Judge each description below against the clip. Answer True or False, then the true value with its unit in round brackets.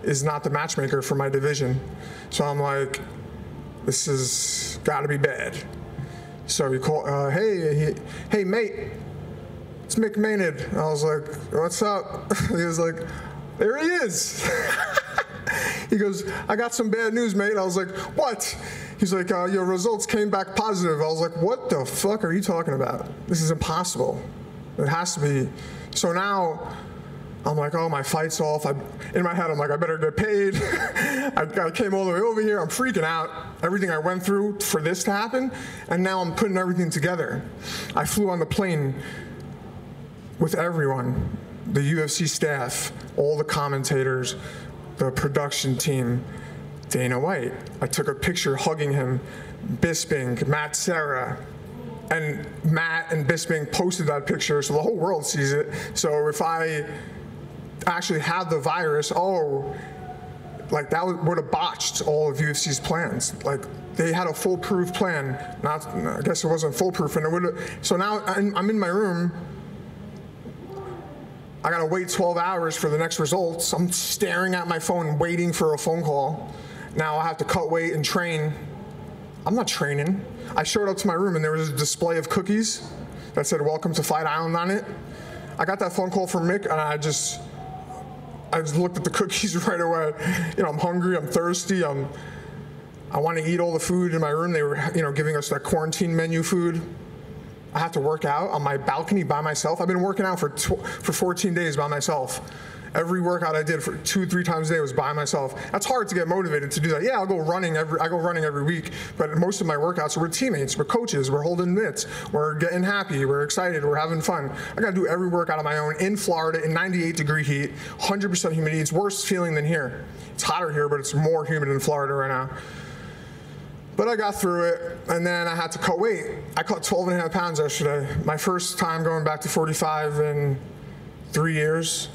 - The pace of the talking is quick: False (195 wpm)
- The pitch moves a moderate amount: True (3.7 semitones)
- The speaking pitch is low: False (165 Hz)